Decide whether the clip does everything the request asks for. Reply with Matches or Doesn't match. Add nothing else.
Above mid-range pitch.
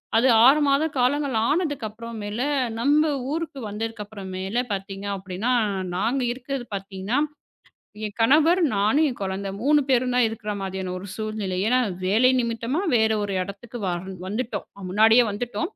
Matches